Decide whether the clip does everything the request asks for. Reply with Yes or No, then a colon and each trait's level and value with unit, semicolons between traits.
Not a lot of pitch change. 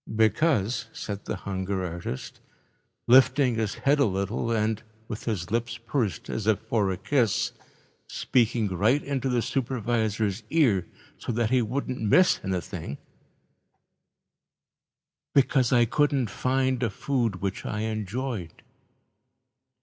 No: average, 4.2 semitones